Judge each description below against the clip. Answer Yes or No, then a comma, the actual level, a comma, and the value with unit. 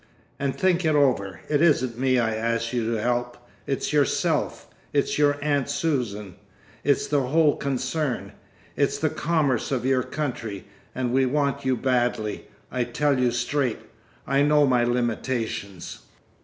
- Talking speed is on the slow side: No, average, 150 wpm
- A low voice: Yes, low, 130 Hz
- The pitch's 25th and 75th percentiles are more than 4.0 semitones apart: No, average, 3.2 semitones